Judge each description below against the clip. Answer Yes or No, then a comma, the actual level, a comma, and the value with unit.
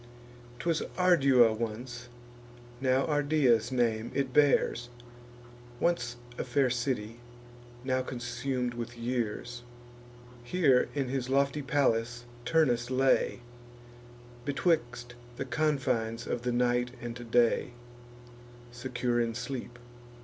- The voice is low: Yes, low, 125 Hz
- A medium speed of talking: No, slow, 100 wpm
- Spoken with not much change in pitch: Yes, narrow, 2.2 semitones